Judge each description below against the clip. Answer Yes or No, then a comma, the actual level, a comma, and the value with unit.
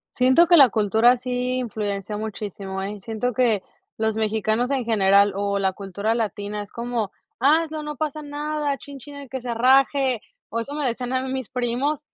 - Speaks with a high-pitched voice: Yes, high, 240 Hz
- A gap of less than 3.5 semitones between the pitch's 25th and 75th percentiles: No, average, 4.4 semitones